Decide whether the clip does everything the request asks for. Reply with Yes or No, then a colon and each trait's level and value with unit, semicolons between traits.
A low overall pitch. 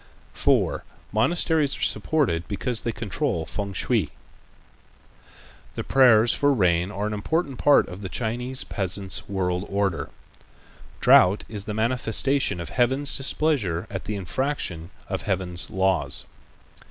Yes: low, 105 Hz